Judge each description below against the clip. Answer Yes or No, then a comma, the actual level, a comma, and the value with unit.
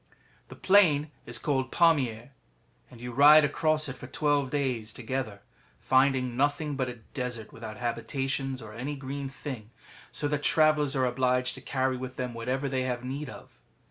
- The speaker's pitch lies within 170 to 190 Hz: No, low, 130 Hz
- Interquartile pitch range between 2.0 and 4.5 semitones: Yes, narrow, 2.6 semitones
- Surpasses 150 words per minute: Yes, average, 175 wpm